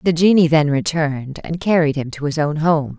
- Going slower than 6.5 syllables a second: Yes, 5.2 syllables/s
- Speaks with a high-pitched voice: No, medium, 155 Hz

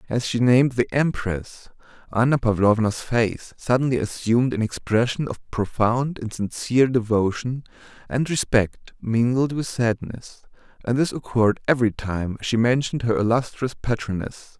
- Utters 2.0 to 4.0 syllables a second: No, 4.7 syllables/s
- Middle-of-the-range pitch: No, low, 120 Hz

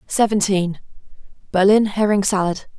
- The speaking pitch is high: Yes, high, 195 Hz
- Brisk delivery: No, slow, 65 wpm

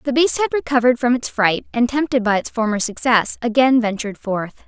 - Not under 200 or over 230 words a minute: Yes, fast, 205 wpm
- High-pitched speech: Yes, high, 240 Hz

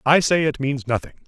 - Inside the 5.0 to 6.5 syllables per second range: Yes, 5.7 syllables/s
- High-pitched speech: No, medium, 140 Hz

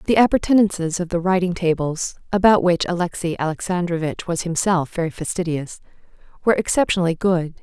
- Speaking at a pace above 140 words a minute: No, slow, 135 wpm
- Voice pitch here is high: No, medium, 175 Hz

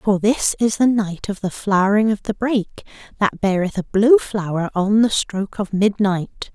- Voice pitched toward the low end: No, high, 205 Hz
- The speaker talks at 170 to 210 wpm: Yes, average, 195 wpm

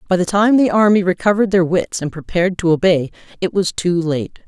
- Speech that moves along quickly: Yes, fast, 215 wpm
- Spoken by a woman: Yes, female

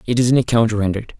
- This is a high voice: No, low, 115 Hz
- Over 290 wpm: No, fast, 250 wpm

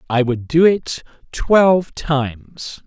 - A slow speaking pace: Yes, slow, 125 wpm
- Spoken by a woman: No, male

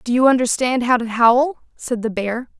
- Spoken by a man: No, female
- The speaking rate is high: Yes, fast, 210 wpm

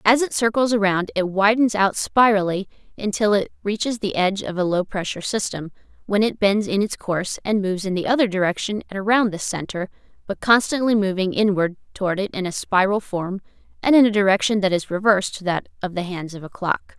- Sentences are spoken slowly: No, fast, 205 wpm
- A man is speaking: No, female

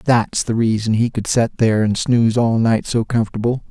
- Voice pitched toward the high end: No, low, 115 Hz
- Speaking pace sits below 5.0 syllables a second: No, 5.4 syllables/s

